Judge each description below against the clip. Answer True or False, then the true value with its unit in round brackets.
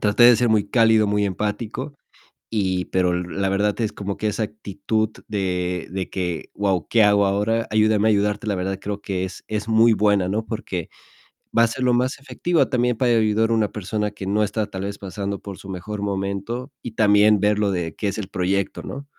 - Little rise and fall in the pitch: True (2.2 semitones)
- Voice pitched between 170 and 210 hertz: False (105 Hz)